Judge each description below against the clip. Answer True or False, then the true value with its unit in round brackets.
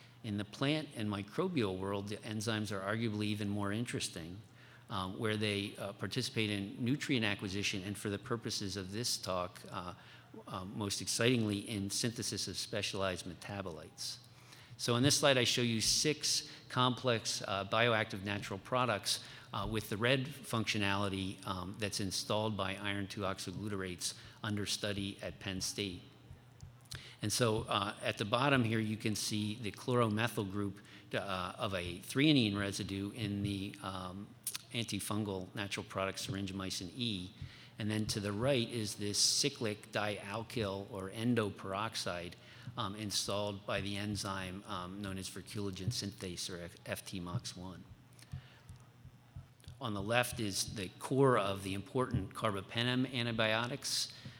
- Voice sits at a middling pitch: False (105 Hz)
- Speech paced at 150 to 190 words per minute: False (140 wpm)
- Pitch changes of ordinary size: True (3.3 semitones)